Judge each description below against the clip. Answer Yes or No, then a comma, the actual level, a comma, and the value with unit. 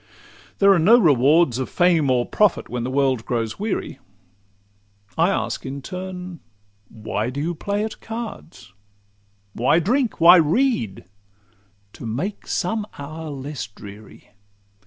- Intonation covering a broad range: Yes, wide, 8.8 semitones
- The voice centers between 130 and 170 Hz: Yes, medium, 140 Hz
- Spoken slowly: Yes, slow, 125 wpm